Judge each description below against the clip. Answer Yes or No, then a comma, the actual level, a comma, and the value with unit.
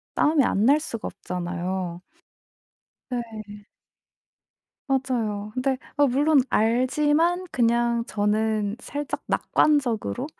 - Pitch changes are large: No, average, 4.8 semitones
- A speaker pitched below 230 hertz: No, high, 235 Hz